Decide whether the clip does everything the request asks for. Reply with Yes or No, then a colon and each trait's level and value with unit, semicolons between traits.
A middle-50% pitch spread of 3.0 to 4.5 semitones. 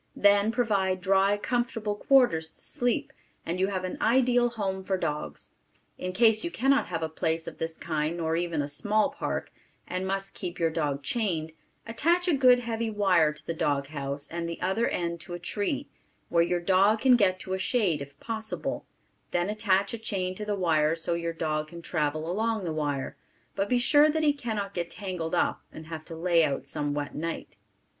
No: average, 5.3 semitones